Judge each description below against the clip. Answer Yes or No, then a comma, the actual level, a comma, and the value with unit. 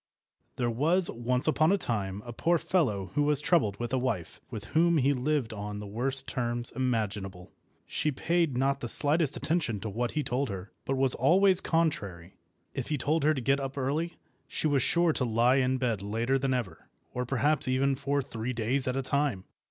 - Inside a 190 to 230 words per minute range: Yes, average, 200 wpm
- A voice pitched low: Yes, low, 130 Hz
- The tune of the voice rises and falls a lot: No, average, 4.3 semitones